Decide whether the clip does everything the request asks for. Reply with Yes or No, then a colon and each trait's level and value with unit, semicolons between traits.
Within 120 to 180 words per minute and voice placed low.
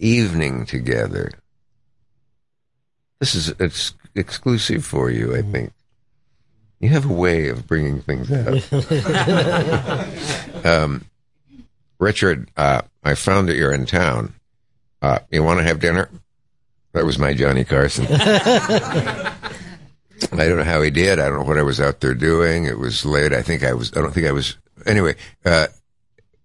Yes: average, 150 wpm; low, 100 Hz